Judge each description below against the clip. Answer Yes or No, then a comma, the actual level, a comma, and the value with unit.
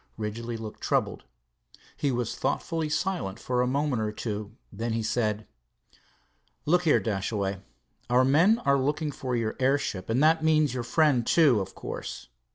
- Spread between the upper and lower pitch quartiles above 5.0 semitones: Yes, wide, 5.4 semitones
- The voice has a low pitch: Yes, low, 125 Hz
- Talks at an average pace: Yes, average, 160 wpm